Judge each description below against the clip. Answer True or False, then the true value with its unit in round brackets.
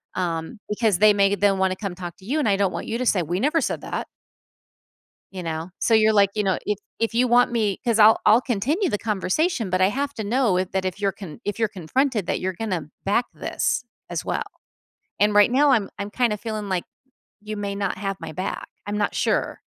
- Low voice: False (205 Hz)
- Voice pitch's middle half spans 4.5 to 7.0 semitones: False (3.2 semitones)